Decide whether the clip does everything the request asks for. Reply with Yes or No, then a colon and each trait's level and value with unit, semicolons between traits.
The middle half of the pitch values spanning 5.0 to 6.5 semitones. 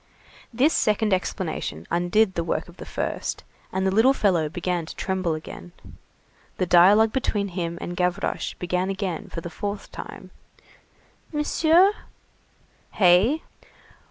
No: average, 3.7 semitones